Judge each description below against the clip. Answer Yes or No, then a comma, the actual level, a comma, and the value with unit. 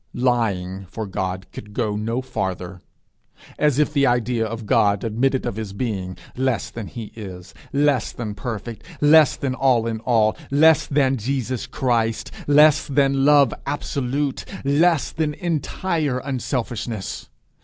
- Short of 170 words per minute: Yes, average, 140 wpm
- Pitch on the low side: Yes, low, 120 Hz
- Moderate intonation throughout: Yes, average, 4.7 semitones